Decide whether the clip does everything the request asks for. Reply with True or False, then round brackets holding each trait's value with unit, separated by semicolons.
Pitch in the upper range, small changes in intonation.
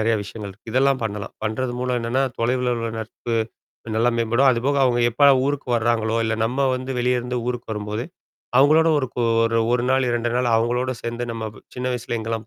False (120 Hz; 2.0 semitones)